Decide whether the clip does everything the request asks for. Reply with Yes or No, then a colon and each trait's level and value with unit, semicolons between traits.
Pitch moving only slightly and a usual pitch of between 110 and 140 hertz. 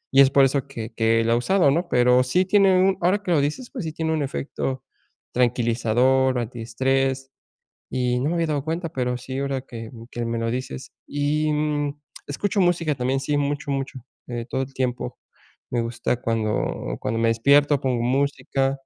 No: average, 3.3 semitones; low, 135 Hz